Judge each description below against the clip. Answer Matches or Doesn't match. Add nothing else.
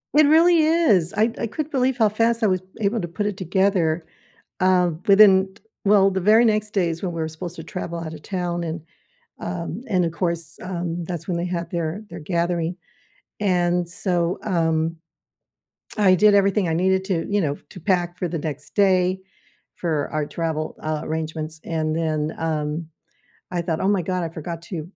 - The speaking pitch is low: Doesn't match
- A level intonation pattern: Doesn't match